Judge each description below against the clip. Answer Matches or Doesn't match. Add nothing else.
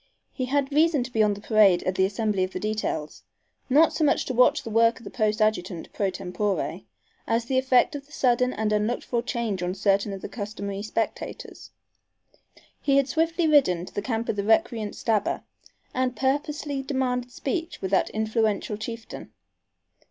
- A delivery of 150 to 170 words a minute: Doesn't match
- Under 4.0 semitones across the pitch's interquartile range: Doesn't match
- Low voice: Doesn't match